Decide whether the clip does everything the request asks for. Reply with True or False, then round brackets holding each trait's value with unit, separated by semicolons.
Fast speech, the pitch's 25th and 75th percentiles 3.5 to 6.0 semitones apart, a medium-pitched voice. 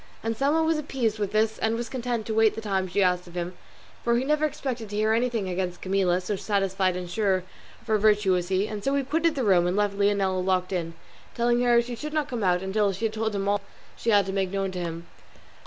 False (250 wpm; 3.9 semitones; 205 Hz)